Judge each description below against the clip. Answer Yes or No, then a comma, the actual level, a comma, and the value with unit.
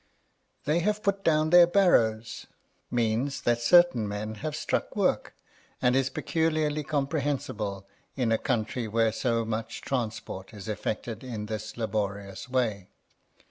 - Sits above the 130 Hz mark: No, low, 120 Hz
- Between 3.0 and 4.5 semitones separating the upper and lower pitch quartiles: No, wide, 5.5 semitones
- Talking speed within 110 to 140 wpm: Yes, slow, 135 wpm